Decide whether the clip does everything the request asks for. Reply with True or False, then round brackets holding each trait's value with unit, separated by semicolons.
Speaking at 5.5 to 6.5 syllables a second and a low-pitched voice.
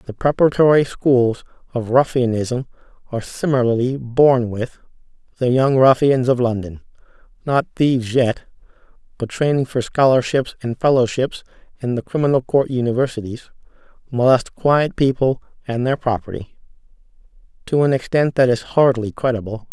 False (5.1 syllables/s; 130 Hz)